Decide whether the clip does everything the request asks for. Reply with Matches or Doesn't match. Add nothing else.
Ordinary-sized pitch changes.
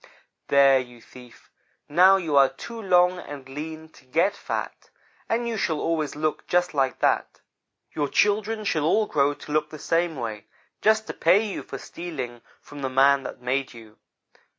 Matches